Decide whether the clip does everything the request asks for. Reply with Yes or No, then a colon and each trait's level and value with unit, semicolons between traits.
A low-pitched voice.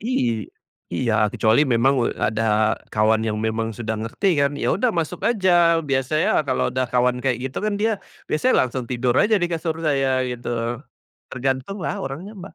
Yes: low, 130 Hz